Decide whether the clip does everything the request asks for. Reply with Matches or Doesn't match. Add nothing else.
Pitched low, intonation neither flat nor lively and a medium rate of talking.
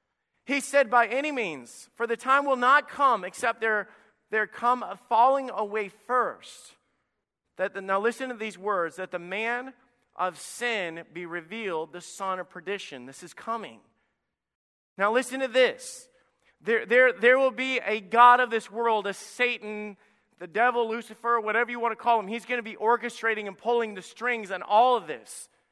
Doesn't match